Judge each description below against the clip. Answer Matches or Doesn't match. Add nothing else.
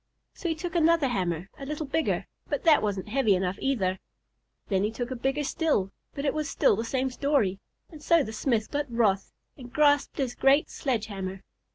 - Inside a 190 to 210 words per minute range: Matches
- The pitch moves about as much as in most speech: Doesn't match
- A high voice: Matches